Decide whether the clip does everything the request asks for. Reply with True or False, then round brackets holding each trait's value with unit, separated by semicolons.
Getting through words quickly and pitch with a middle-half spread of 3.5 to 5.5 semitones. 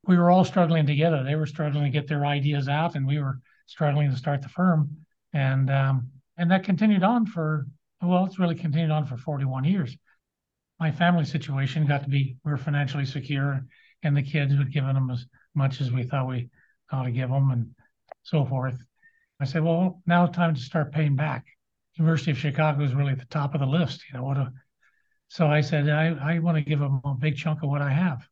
False (225 wpm; 3.0 semitones)